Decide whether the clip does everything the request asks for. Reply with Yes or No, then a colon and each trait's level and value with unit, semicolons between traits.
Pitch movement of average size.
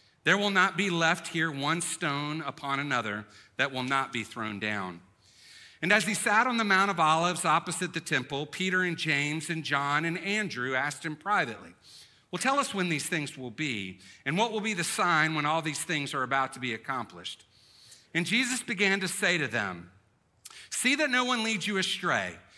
No: wide, 5.9 semitones